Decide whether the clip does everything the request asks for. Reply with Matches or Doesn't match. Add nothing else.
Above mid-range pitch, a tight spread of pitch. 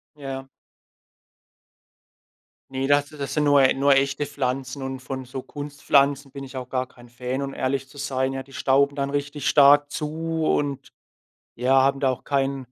Doesn't match